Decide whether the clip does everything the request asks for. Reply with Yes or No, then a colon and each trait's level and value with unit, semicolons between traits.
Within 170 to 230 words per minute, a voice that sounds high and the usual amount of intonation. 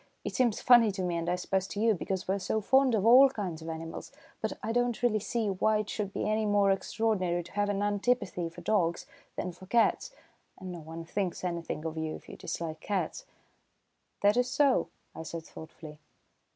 Yes: fast, 205 wpm; high, 195 Hz; average, 4.3 semitones